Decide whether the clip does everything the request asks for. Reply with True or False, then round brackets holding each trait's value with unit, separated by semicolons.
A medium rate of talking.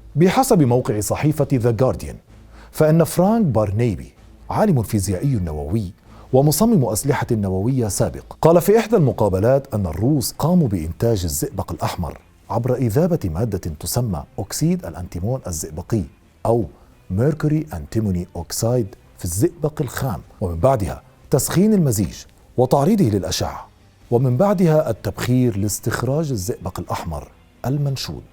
True (110 wpm)